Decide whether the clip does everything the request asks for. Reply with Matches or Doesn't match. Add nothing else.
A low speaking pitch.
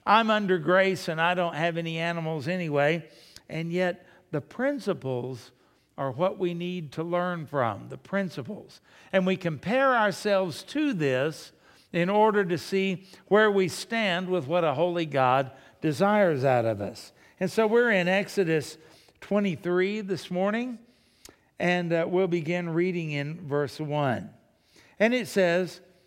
Doesn't match